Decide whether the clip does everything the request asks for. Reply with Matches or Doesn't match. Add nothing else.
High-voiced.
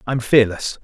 Doesn't match